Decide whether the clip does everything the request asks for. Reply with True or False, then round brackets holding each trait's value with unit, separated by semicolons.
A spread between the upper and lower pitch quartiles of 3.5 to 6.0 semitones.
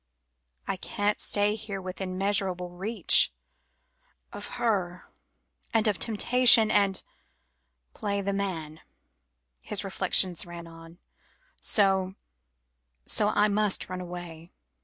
False (2.6 semitones)